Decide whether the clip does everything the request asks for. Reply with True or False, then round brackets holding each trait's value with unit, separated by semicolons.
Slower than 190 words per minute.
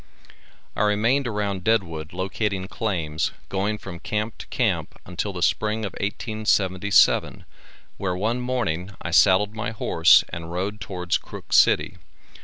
True (135 wpm)